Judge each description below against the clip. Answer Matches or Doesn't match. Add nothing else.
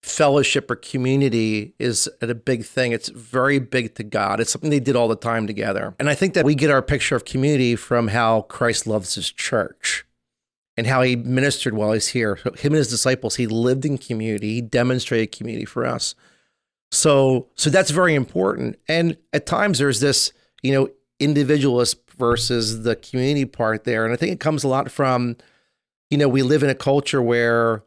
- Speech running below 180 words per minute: Doesn't match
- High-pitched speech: Doesn't match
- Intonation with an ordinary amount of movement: Matches